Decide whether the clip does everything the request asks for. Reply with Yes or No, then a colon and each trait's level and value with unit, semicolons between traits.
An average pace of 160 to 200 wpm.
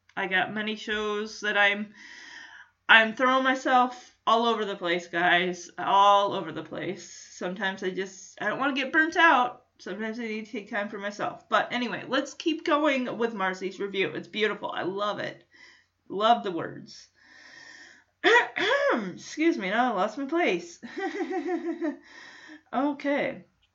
No: average, 150 wpm